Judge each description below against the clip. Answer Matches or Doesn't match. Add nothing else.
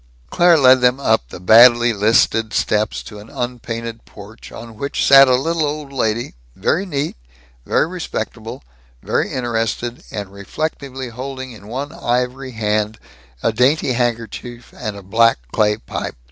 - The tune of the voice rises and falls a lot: Doesn't match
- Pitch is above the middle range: Doesn't match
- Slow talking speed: Doesn't match